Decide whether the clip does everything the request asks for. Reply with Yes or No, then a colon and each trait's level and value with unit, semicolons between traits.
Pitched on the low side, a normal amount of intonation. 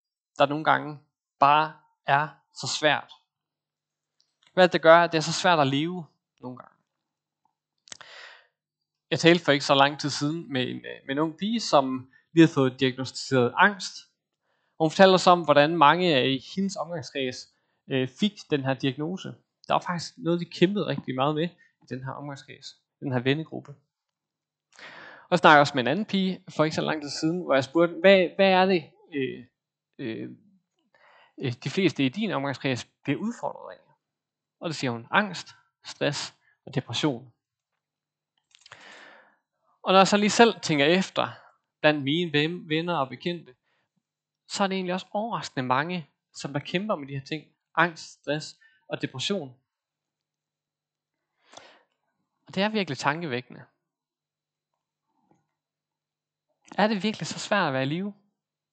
No: medium, 155 Hz; average, 4.6 semitones